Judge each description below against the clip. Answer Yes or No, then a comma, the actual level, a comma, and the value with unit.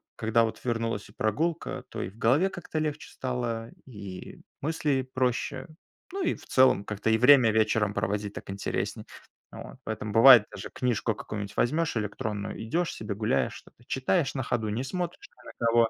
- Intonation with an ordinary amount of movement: Yes, average, 3.8 semitones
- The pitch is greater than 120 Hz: No, low, 115 Hz